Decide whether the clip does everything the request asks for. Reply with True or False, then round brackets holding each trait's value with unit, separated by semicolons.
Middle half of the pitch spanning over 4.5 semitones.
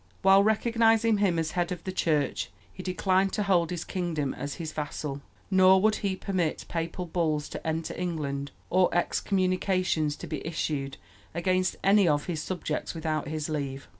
False (3.5 semitones)